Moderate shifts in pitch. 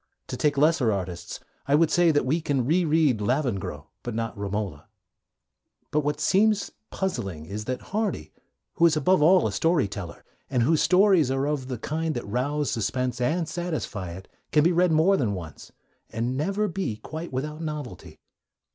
No: wide, 6.3 semitones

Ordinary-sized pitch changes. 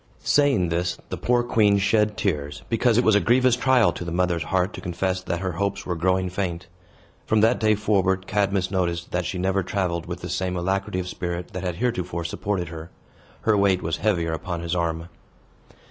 Yes: average, 3.0 semitones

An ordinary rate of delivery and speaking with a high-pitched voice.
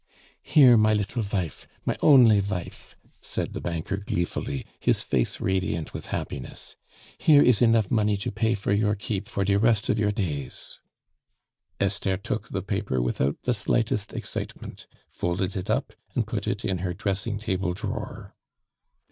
No: average, 155 wpm; low, 100 Hz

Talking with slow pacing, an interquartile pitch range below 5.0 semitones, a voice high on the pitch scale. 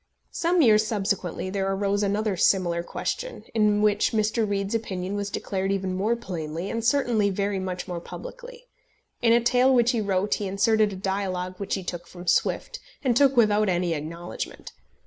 No: average, 175 wpm; average, 3.3 semitones; high, 200 Hz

